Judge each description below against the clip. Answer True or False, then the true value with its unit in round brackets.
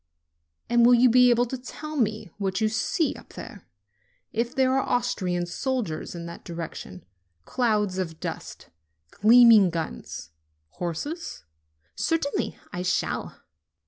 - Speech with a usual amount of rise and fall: False (6.0 semitones)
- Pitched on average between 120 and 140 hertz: False (220 Hz)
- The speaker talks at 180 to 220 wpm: False (135 wpm)